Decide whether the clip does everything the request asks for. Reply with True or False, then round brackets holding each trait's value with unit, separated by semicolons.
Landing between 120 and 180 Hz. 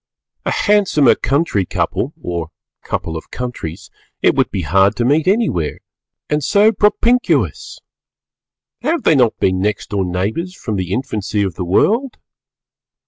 False (110 Hz)